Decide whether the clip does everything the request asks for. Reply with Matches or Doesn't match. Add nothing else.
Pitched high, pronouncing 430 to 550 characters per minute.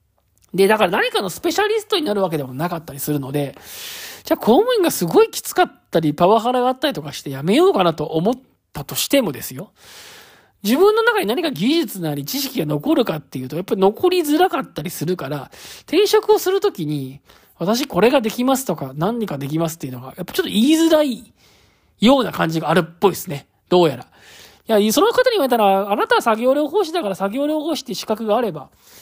Matches